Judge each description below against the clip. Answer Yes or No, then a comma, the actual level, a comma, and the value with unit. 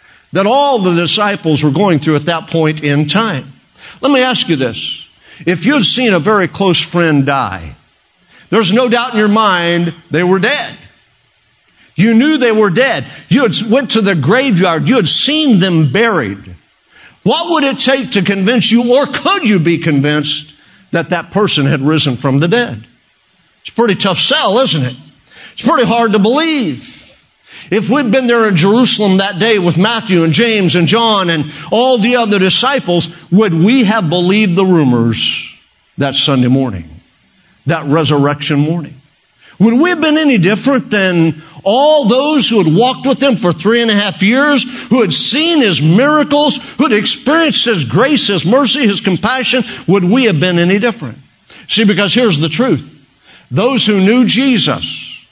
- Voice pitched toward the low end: No, high, 205 Hz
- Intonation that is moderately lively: No, wide, 6.7 semitones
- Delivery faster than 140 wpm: Yes, average, 175 wpm